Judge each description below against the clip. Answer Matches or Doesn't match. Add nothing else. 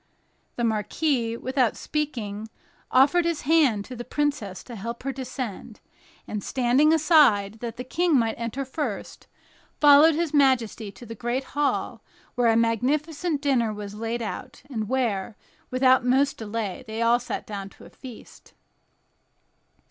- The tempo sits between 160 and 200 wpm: Doesn't match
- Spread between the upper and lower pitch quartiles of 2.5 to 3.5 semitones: Doesn't match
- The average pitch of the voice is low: Doesn't match